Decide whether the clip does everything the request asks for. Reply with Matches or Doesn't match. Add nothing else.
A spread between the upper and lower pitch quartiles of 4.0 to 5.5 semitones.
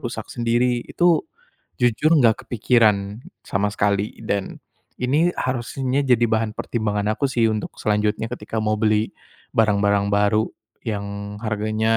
Doesn't match